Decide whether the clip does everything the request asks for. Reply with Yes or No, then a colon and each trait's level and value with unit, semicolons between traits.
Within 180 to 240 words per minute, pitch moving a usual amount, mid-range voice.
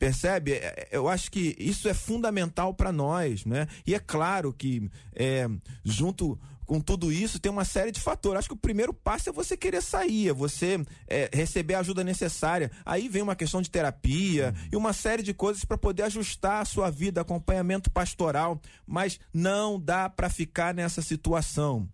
Yes: fast, 185 wpm; average, 4.6 semitones; medium, 175 Hz